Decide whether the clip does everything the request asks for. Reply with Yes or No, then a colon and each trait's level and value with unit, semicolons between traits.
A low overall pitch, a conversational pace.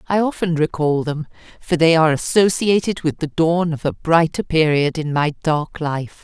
No: medium, 160 Hz; average, 185 wpm